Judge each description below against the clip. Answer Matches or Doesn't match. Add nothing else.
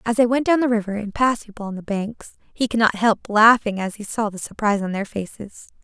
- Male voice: Doesn't match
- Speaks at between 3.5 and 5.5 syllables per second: Doesn't match